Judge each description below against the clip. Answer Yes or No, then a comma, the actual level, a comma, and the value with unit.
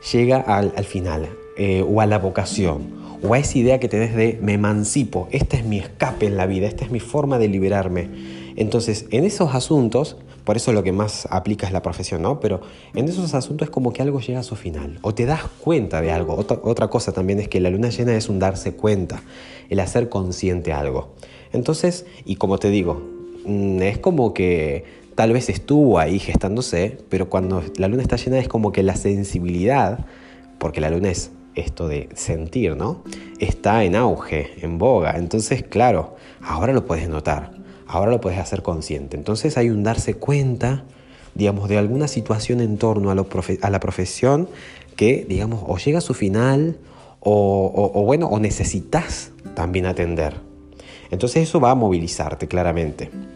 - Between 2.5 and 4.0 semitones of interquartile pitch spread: No, average, 5.2 semitones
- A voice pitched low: Yes, low, 100 Hz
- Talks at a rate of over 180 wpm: Yes, fast, 190 wpm